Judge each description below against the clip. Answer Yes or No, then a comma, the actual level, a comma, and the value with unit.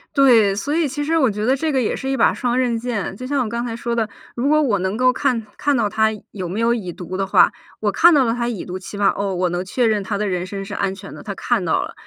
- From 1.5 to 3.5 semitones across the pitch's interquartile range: No, average, 4.5 semitones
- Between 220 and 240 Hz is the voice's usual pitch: Yes, high, 225 Hz